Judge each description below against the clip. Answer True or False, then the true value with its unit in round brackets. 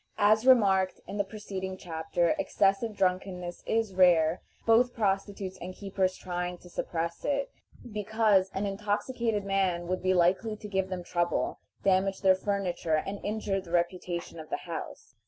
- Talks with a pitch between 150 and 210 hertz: True (190 Hz)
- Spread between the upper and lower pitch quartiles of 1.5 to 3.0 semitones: True (2.5 semitones)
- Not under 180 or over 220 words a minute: False (155 wpm)